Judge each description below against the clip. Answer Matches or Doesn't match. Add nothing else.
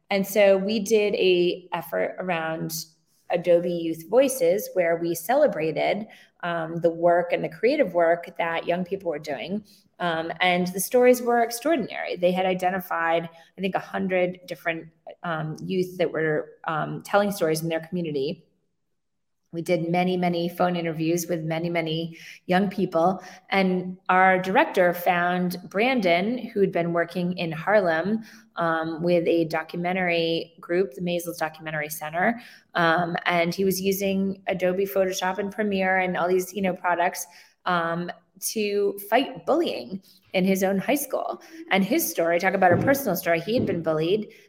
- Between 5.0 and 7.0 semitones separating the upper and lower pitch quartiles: Doesn't match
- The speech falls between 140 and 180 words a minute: Matches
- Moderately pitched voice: Matches